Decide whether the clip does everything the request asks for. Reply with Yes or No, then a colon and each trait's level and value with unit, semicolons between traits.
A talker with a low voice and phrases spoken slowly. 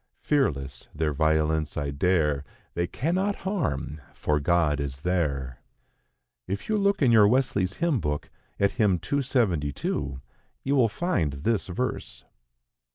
Yes: very low, 85 Hz; slow, 130 wpm